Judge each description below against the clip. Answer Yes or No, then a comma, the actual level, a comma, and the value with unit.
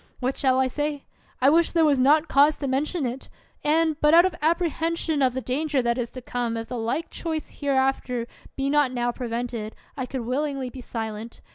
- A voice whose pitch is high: Yes, very high, 270 Hz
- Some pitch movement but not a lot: Yes, average, 3.6 semitones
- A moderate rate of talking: No, fast, 210 wpm